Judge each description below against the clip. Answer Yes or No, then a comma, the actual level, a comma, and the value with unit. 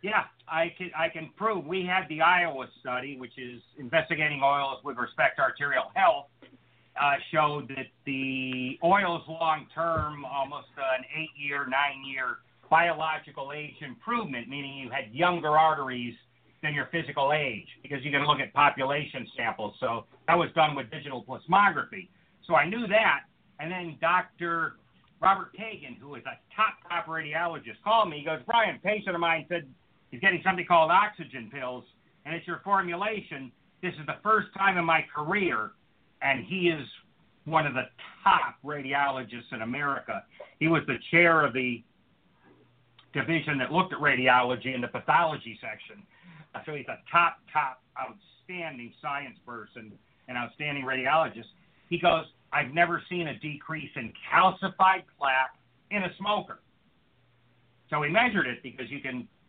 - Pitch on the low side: No, medium, 150 Hz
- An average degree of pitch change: Yes, average, 4.7 semitones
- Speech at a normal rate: Yes, average, 160 wpm